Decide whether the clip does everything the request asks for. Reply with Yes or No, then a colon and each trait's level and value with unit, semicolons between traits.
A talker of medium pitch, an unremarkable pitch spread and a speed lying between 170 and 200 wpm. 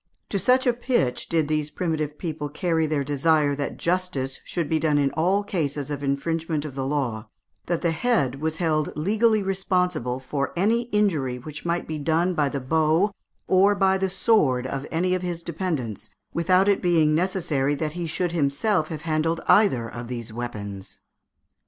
Yes: medium, 160 Hz; average, 4.6 semitones; average, 175 wpm